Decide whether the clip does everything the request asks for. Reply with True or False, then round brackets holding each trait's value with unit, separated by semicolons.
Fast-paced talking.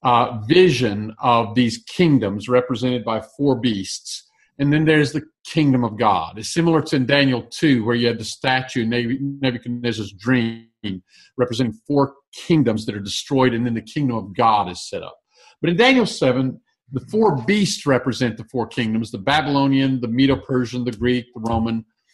False (175 wpm)